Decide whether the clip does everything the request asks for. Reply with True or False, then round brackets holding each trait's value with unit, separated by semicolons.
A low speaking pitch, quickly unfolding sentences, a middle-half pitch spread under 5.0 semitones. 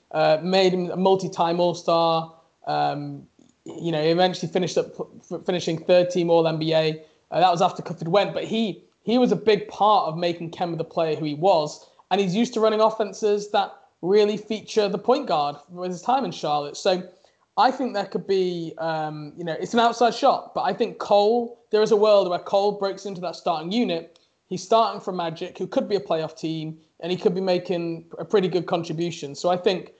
False (180 Hz; 210 wpm; 3.9 semitones)